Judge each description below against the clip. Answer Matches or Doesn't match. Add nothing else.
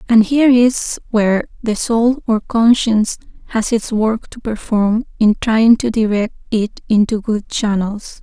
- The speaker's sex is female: Matches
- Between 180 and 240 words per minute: Doesn't match